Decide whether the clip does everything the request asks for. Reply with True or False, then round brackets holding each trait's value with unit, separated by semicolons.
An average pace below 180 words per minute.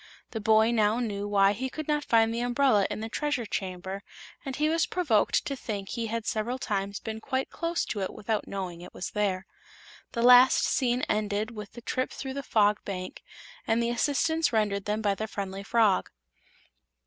False (195 wpm)